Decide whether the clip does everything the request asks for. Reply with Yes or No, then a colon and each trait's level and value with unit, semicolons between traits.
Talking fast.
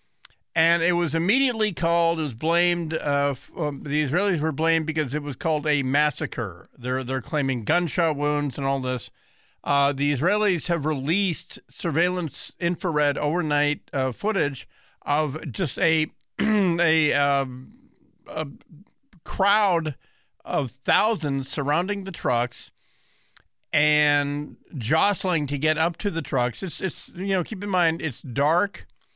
No: average, 140 wpm